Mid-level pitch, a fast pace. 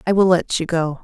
Yes: medium, 175 Hz; fast, 290 wpm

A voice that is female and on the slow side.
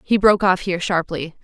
No: female; fast, 210 wpm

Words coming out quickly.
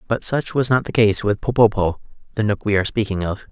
Yes: fast, 240 wpm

